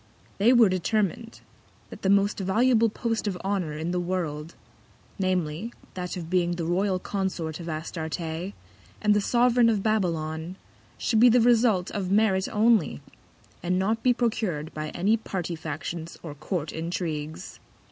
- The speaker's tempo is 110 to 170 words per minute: Yes, average, 150 wpm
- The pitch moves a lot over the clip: No, average, 4.7 semitones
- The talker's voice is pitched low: No, medium, 185 Hz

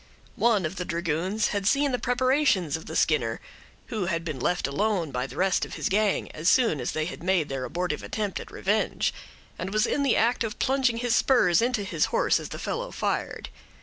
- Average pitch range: No, wide, 6.2 semitones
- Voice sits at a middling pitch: No, high, 195 Hz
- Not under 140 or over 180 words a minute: No, fast, 205 wpm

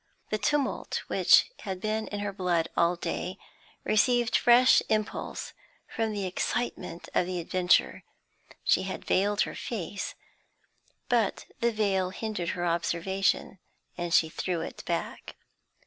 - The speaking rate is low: Yes, slow, 130 wpm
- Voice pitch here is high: Yes, high, 195 Hz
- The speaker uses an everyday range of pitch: Yes, average, 3.5 semitones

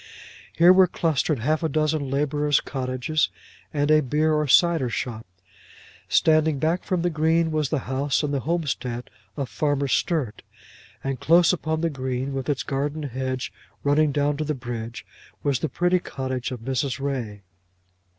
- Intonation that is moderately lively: Yes, average, 3.1 semitones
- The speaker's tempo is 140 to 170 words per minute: Yes, average, 160 wpm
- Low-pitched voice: No, medium, 145 Hz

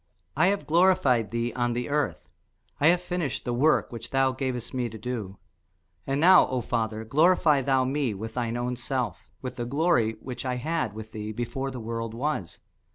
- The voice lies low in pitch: Yes, low, 125 Hz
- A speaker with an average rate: Yes, average, 190 wpm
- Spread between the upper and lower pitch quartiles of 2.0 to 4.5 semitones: Yes, average, 3.9 semitones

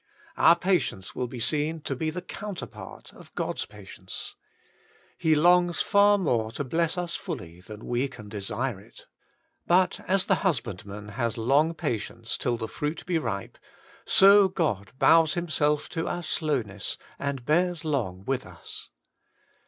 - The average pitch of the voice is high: No, medium, 150 Hz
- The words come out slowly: No, average, 150 wpm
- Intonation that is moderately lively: No, wide, 7.3 semitones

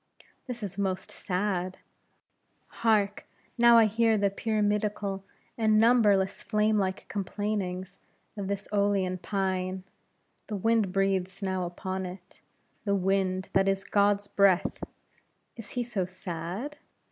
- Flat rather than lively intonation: Yes, narrow, 2.1 semitones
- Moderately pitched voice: No, high, 200 Hz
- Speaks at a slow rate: Yes, slow, 125 wpm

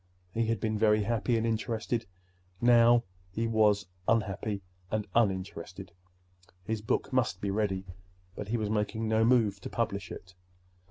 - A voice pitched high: No, low, 110 Hz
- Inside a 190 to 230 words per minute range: No, average, 150 wpm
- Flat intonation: Yes, narrow, 2.3 semitones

